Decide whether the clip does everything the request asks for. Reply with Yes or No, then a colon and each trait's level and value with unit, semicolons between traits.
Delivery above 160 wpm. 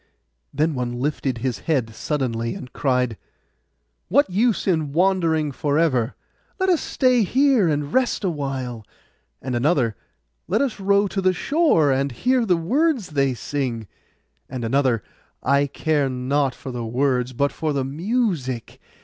No: average, 150 wpm